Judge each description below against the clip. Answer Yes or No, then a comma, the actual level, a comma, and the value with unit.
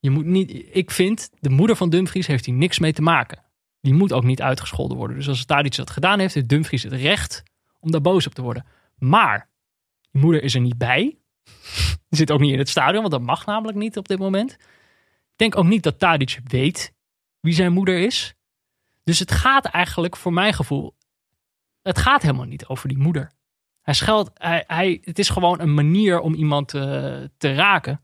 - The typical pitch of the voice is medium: Yes, medium, 160 Hz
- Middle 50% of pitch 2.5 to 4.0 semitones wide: No, average, 5.3 semitones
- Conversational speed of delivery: No, fast, 210 wpm